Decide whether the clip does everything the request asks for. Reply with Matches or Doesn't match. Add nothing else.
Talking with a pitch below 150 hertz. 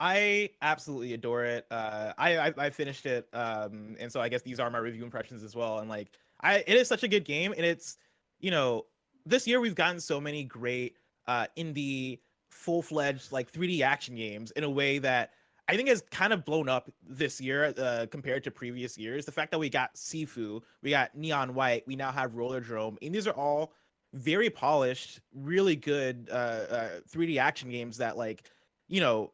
Matches